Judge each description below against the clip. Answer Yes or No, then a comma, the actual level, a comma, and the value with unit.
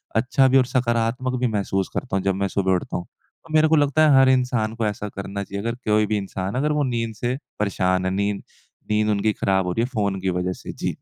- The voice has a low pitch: Yes, low, 110 Hz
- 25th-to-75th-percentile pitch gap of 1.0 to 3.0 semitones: No, average, 4.6 semitones